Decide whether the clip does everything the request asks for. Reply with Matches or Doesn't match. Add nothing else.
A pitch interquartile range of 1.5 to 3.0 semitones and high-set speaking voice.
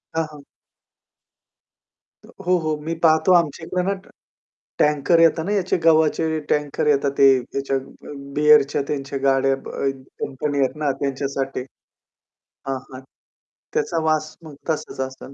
Doesn't match